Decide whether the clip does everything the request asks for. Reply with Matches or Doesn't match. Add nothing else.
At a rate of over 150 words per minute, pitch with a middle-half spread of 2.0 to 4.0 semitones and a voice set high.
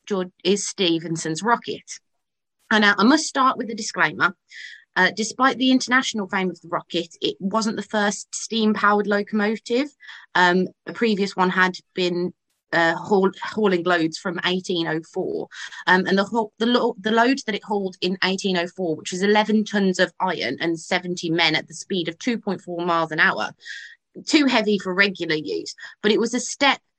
Matches